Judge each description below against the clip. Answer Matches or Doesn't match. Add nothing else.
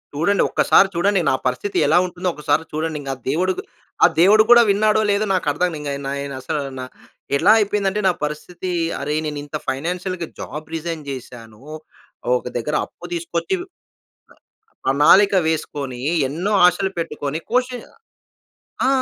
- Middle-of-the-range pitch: Matches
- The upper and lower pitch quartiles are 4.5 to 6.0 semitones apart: Matches